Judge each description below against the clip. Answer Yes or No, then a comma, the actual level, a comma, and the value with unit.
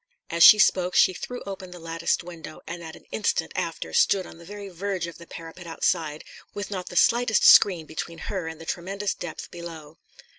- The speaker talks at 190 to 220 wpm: Yes, average, 200 wpm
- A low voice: No, medium, 175 Hz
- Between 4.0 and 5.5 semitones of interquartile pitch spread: No, average, 3.0 semitones